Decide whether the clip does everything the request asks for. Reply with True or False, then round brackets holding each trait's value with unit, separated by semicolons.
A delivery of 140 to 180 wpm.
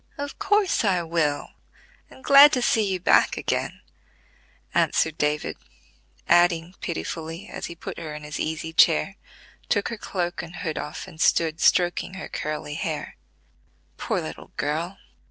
True (150 wpm)